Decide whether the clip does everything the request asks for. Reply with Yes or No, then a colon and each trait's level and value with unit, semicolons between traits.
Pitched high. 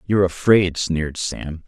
No: very low, 85 Hz